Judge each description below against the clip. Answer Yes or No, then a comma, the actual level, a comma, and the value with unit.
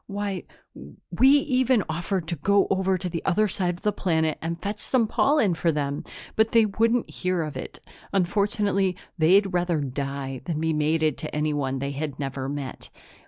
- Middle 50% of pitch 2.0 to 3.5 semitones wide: No, average, 5.0 semitones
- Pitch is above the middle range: No, medium, 175 Hz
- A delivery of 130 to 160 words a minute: No, average, 175 wpm